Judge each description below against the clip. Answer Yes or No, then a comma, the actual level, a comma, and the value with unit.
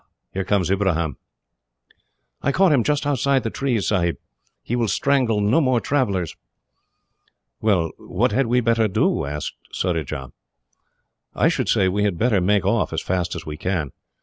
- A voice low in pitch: Yes, low, 105 Hz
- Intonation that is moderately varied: No, wide, 5.8 semitones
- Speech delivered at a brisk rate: No, average, 160 wpm